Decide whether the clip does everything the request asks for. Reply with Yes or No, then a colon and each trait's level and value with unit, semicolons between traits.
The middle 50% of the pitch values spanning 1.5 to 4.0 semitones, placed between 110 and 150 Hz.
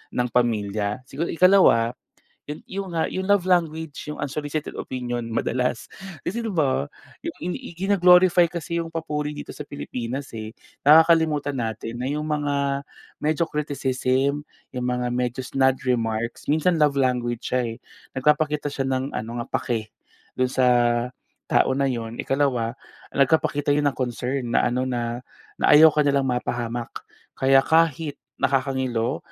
Yes: average, 3.7 semitones; low, 135 Hz